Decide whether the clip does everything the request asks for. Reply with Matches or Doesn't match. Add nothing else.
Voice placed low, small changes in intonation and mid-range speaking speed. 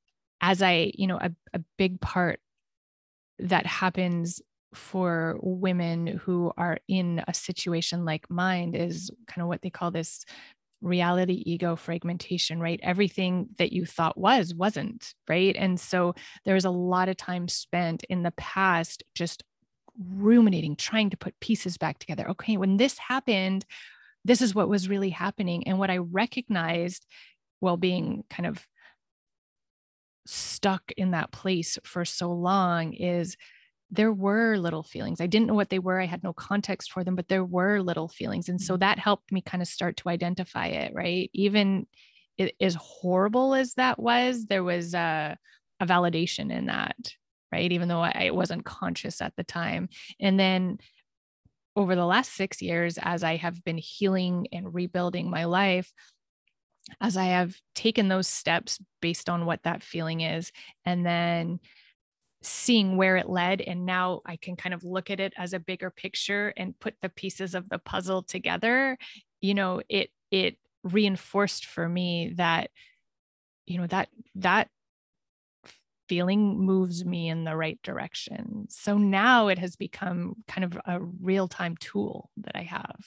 Doesn't match